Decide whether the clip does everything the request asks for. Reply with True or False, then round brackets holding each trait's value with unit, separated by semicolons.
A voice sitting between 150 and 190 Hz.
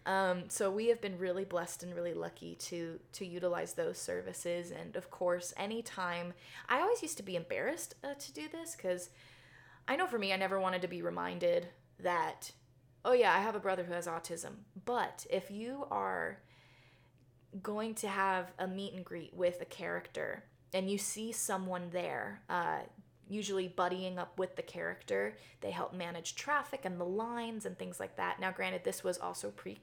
True (185 Hz)